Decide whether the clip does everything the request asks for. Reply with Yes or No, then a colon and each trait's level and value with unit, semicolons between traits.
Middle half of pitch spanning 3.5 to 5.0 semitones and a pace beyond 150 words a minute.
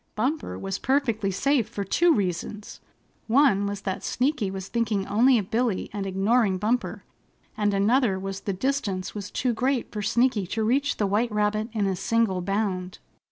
Yes: average, 3.9 semitones; average, 170 wpm